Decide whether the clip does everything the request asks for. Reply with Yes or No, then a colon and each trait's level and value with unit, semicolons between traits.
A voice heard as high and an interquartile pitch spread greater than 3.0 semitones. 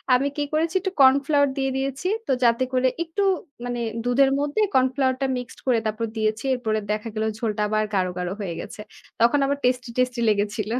Yes: very high, 250 Hz; average, 4.1 semitones